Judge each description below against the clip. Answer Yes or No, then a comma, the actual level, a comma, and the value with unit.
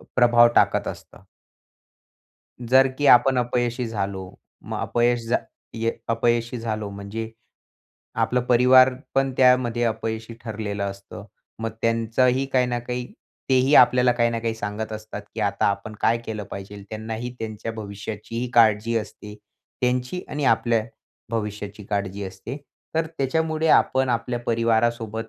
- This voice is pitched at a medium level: No, low, 115 Hz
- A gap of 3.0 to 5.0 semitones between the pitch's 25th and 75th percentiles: No, narrow, 2.4 semitones